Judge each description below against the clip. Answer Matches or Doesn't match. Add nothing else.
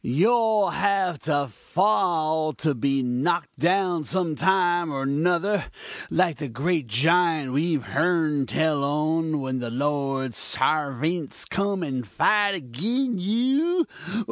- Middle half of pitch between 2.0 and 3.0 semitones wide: Doesn't match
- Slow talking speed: Matches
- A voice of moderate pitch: Matches